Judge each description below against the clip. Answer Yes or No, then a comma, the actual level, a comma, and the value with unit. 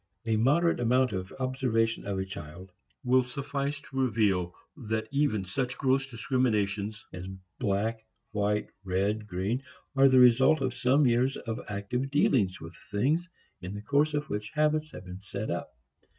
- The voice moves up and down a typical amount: Yes, average, 4.8 semitones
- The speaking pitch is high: No, low, 115 Hz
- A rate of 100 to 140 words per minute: No, average, 160 wpm